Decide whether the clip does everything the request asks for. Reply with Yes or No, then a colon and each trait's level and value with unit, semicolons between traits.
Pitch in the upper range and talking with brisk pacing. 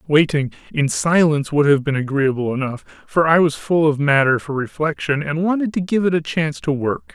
No: medium, 150 Hz; fast, 210 wpm